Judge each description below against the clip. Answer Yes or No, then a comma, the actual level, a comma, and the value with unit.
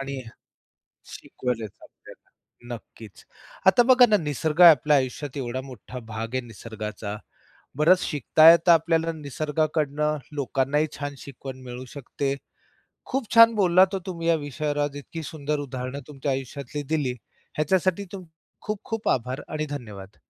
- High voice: No, medium, 145 Hz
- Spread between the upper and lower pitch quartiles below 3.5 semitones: No, average, 4.2 semitones